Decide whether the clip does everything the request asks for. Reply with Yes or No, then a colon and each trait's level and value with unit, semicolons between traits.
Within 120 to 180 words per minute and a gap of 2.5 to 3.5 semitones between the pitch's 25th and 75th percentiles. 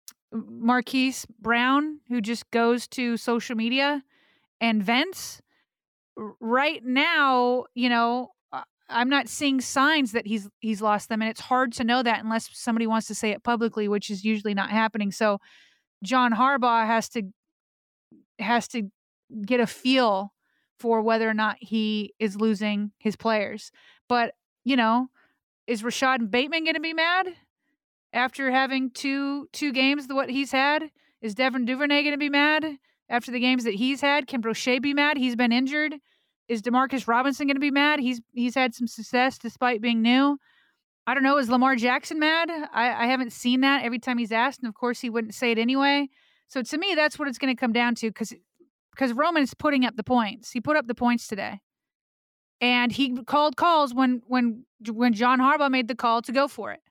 No: average, 190 wpm; average, 3.2 semitones